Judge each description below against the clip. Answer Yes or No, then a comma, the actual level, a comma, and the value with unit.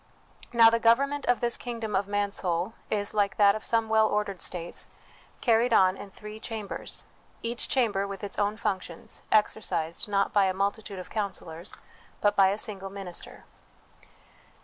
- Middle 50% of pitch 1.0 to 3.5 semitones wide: Yes, narrow, 2.4 semitones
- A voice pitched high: Yes, high, 205 Hz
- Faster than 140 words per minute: Yes, average, 170 wpm